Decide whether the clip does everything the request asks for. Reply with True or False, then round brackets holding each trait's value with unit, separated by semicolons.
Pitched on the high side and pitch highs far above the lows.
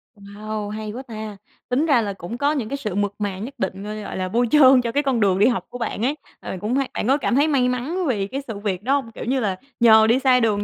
False (230 Hz; 4.2 semitones)